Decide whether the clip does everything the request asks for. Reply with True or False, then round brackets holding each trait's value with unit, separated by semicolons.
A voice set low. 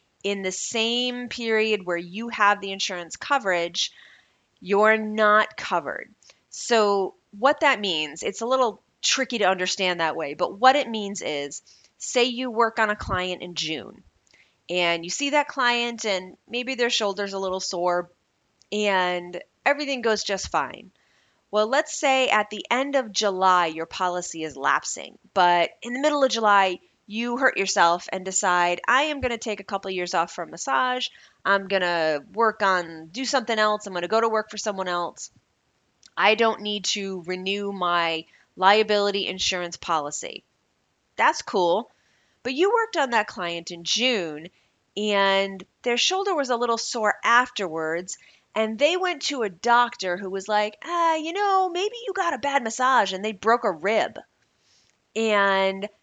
False (210 Hz)